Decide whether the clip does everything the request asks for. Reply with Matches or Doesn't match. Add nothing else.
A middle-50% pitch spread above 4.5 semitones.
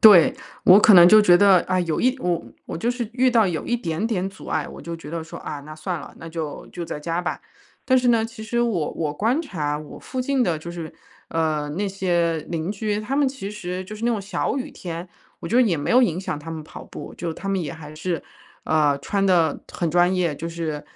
Matches